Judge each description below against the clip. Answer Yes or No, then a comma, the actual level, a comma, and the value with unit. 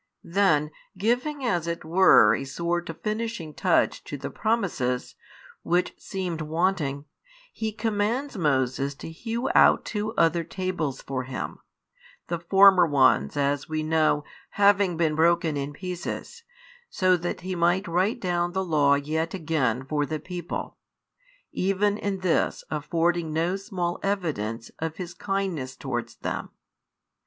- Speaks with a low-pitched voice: No, medium, 170 Hz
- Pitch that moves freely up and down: No, average, 4.2 semitones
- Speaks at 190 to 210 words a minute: No, average, 140 wpm